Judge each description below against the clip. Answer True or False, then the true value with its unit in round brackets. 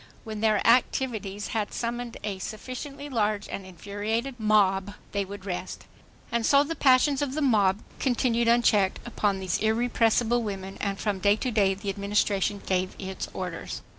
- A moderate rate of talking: True (160 wpm)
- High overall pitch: True (215 Hz)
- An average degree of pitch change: True (3.4 semitones)